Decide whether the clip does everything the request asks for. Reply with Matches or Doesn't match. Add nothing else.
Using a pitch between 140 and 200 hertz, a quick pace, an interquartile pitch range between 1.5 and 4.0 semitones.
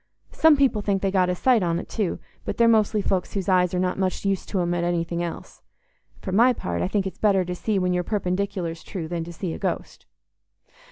Matches